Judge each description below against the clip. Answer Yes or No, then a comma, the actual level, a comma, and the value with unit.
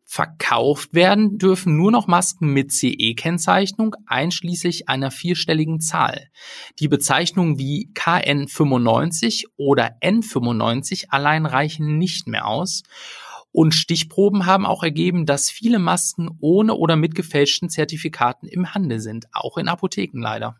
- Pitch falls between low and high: Yes, medium, 165 Hz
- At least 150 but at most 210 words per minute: No, slow, 125 wpm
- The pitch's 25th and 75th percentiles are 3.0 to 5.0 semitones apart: Yes, average, 4.6 semitones